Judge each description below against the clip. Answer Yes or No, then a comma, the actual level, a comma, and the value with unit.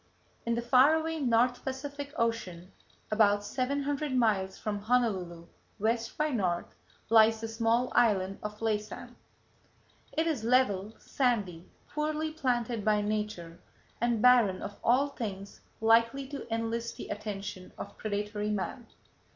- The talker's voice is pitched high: Yes, high, 225 Hz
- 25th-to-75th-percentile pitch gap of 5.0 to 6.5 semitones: No, average, 3.5 semitones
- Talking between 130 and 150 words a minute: Yes, slow, 135 wpm